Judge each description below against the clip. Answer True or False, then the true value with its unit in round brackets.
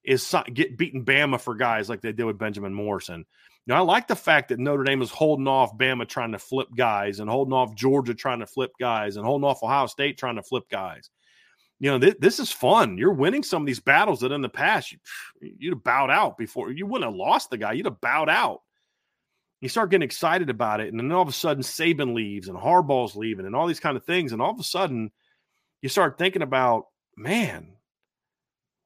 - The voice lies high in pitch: False (130 Hz)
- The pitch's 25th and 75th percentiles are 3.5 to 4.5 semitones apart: True (4.1 semitones)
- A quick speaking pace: True (230 wpm)